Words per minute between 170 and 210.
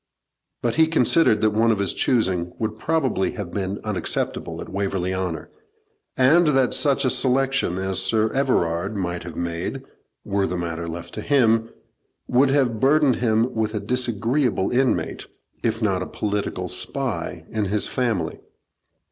No: average, 155 wpm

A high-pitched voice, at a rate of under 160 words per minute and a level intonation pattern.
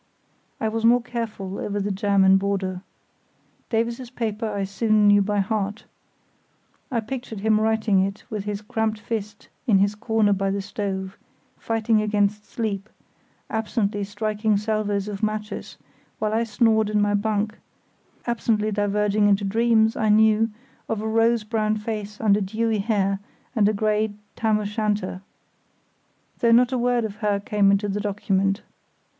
Yes: high, 210 Hz; average, 150 wpm; narrow, 1.6 semitones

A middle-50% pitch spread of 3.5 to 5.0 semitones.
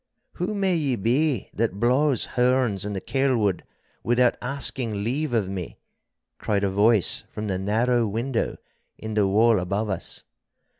Yes: average, 4.1 semitones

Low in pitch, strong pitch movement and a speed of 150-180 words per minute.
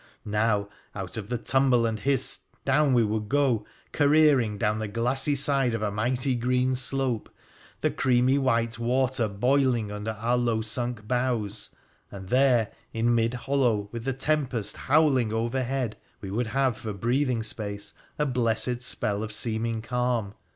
No: low, 120 Hz; average, 3.1 semitones; average, 160 wpm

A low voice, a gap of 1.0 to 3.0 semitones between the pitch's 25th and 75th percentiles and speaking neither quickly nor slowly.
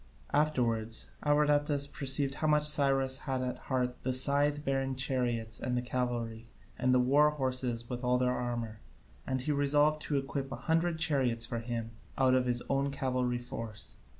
Yes: low, 130 Hz; narrow, 2.6 semitones; average, 165 wpm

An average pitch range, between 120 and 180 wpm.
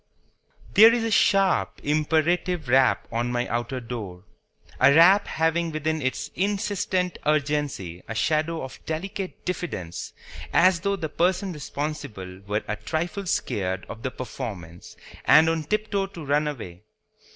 No: wide, 6.8 semitones; average, 140 wpm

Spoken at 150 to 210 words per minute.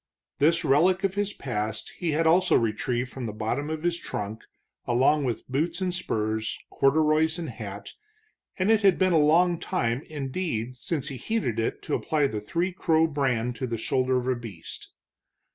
Yes: average, 180 wpm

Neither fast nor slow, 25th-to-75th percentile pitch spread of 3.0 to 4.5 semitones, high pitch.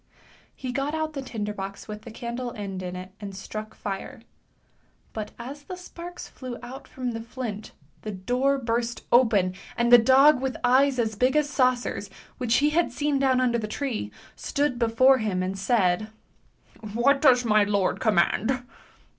Yes: average, 175 wpm; average, 3.9 semitones; high, 240 Hz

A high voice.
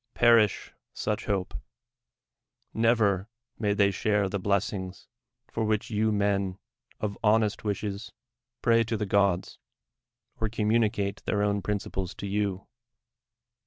No: low, 105 Hz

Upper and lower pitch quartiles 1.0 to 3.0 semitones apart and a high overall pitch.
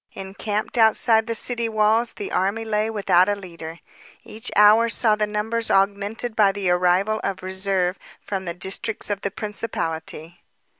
Yes: average, 2.7 semitones; high, 205 Hz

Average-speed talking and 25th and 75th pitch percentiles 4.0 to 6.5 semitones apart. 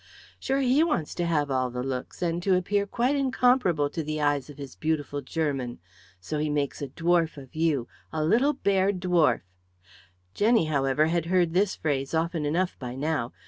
Yes: average, 185 wpm; average, 4.5 semitones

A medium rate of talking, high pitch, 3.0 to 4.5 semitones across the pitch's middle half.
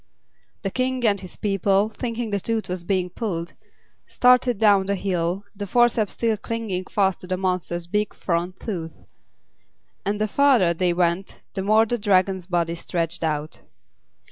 Yes: average, 155 wpm; high, 195 Hz; average, 3.4 semitones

